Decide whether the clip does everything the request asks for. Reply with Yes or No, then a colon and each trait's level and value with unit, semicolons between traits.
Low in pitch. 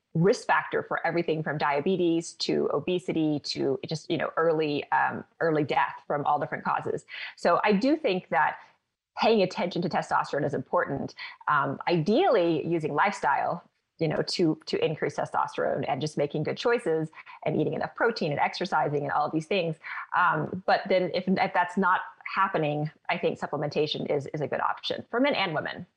No: medium, 170 Hz